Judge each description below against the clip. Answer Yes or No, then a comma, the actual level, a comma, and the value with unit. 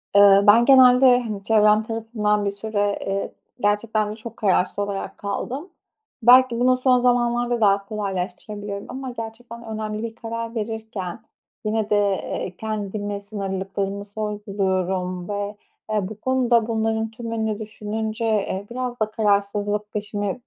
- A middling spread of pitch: No, narrow, 2.2 semitones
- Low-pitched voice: No, high, 215 Hz